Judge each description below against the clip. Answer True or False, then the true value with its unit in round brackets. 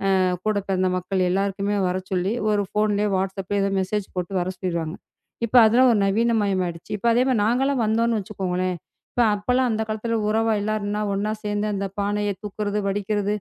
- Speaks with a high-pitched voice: True (205 Hz)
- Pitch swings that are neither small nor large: False (2.0 semitones)